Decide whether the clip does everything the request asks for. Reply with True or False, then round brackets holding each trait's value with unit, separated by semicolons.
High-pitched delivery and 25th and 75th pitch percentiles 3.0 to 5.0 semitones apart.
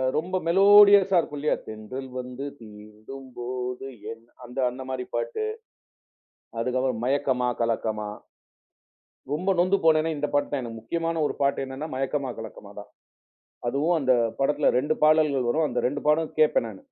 False (135 Hz; 4.1 semitones)